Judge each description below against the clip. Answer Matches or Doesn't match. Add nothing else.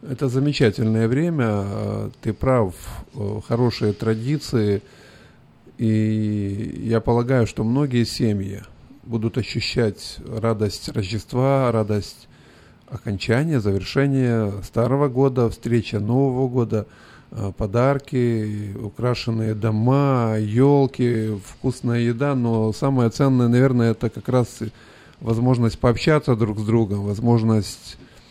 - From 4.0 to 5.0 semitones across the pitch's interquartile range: Doesn't match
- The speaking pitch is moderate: Doesn't match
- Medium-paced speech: Doesn't match